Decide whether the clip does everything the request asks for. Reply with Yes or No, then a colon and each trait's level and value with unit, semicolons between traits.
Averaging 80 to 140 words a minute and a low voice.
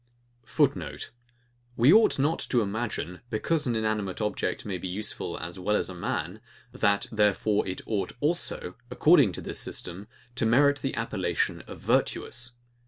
No: average, 155 wpm; low, 110 Hz